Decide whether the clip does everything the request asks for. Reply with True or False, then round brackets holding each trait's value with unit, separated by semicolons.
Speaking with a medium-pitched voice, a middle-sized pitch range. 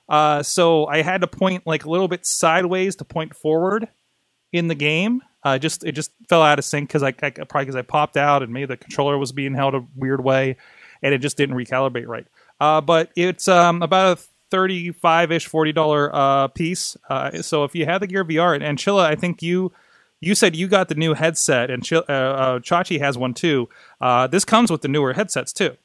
True (155 Hz; 3.9 semitones)